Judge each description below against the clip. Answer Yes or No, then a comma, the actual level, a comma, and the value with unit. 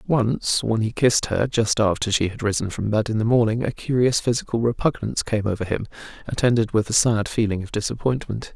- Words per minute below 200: No, fast, 205 wpm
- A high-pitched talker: No, low, 110 Hz